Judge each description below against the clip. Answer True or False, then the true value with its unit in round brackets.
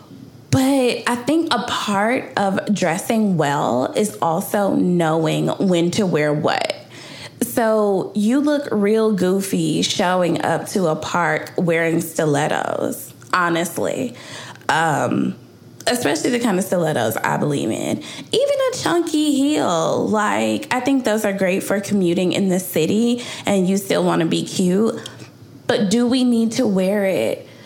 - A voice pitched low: False (200 Hz)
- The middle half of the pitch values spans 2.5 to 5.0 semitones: False (5.4 semitones)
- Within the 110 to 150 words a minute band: True (140 wpm)